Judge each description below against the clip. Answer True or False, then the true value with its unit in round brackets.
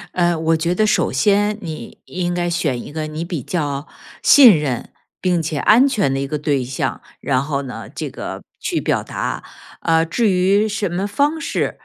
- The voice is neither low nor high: True (170 Hz)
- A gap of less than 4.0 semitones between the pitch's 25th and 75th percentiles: False (5.5 semitones)